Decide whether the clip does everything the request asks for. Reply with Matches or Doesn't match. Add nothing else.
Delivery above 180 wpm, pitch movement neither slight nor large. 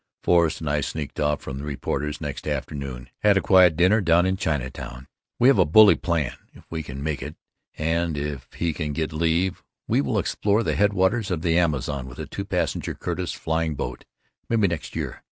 Matches